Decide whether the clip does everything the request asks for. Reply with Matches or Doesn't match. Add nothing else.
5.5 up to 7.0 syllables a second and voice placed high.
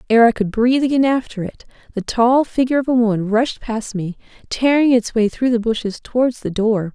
Matches